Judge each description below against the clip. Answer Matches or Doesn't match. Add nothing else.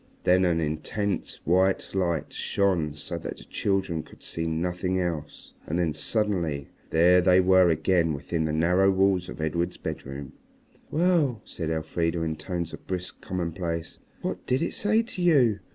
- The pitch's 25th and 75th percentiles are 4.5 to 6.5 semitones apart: Doesn't match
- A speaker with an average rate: Matches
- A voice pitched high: Doesn't match